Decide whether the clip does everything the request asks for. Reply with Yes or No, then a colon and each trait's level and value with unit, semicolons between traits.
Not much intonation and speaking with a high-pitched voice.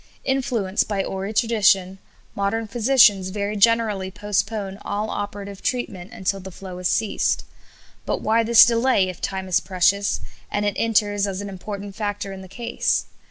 Yes: narrow, 2.3 semitones; high, 205 Hz